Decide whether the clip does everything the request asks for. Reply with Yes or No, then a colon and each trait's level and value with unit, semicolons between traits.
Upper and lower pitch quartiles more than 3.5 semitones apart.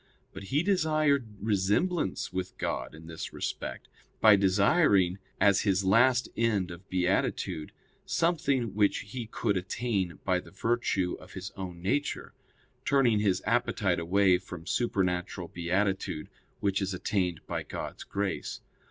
Yes: average, 4.1 semitones